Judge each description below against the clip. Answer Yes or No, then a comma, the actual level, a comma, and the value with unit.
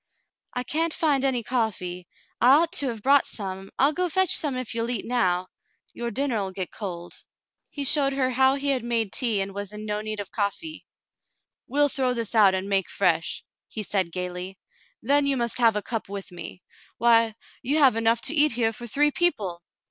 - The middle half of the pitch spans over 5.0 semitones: Yes, wide, 5.5 semitones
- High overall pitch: Yes, high, 230 Hz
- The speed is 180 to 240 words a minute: Yes, fast, 205 wpm